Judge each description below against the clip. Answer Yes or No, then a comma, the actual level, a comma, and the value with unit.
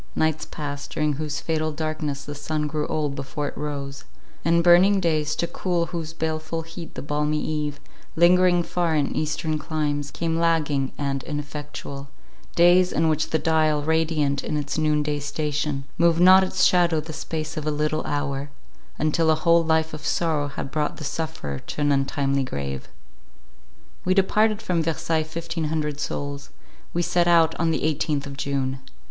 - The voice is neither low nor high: Yes, medium, 155 Hz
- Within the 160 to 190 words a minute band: Yes, average, 170 wpm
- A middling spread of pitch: No, narrow, 2.0 semitones